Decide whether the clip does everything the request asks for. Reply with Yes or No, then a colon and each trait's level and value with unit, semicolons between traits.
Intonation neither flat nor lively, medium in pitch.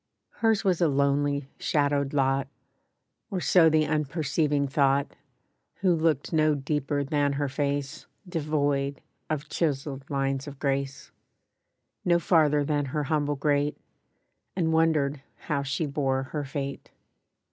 No: narrow, 1.9 semitones; medium, 145 Hz